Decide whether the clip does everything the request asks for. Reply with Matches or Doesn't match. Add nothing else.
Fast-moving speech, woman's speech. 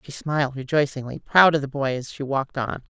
Matches